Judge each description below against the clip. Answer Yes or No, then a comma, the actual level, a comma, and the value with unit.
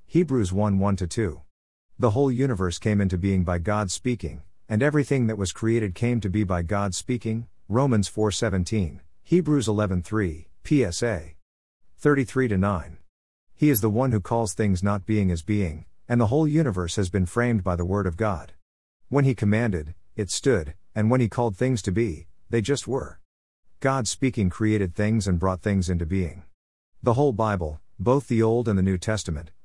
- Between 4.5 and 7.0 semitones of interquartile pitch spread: Yes, average, 4.9 semitones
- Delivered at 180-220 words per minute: Yes, average, 185 wpm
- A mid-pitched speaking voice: No, low, 105 Hz